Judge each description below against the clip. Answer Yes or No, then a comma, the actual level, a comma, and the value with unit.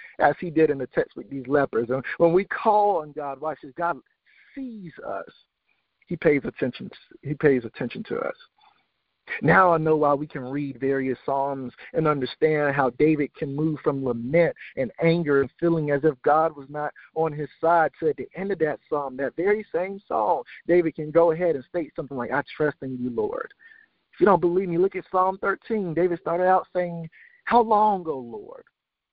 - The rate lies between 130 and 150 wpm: No, fast, 205 wpm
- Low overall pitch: No, medium, 160 Hz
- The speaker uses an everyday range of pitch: Yes, average, 4.6 semitones